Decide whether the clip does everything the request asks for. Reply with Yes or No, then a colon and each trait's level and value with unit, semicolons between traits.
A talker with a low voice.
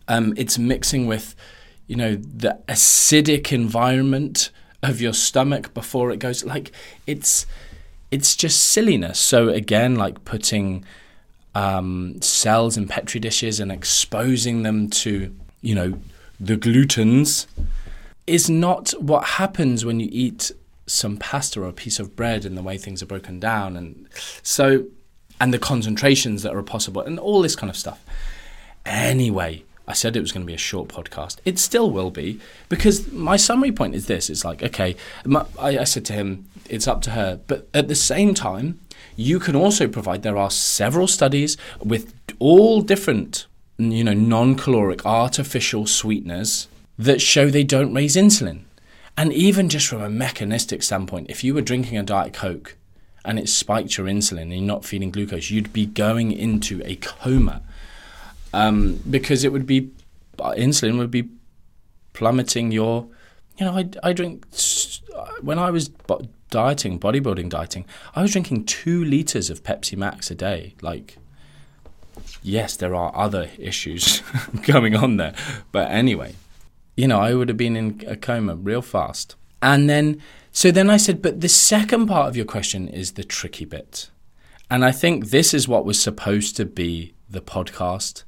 Yes: low, 115 Hz